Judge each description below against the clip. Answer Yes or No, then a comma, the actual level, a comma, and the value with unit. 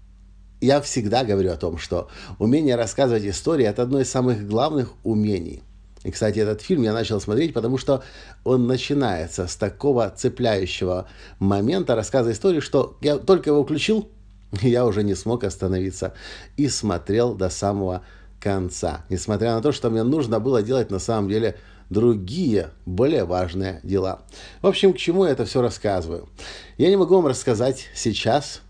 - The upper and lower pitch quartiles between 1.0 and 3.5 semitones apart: No, average, 5.1 semitones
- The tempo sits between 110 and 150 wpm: No, fast, 160 wpm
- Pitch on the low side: Yes, low, 110 Hz